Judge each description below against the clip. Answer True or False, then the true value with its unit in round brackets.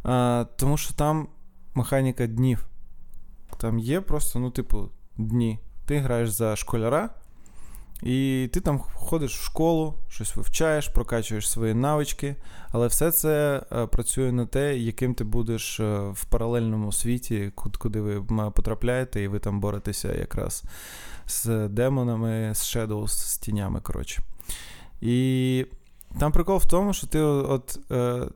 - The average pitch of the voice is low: True (120 Hz)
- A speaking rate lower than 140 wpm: True (130 wpm)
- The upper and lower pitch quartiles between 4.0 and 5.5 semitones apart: True (4.3 semitones)